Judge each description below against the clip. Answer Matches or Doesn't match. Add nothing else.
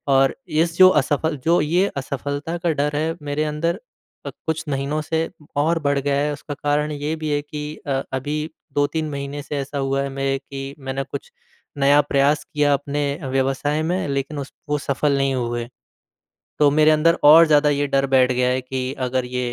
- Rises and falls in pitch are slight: Matches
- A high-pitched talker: Doesn't match